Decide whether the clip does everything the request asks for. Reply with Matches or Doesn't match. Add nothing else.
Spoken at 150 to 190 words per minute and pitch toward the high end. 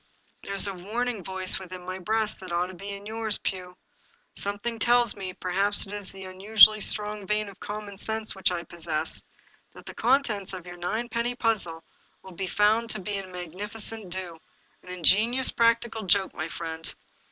Matches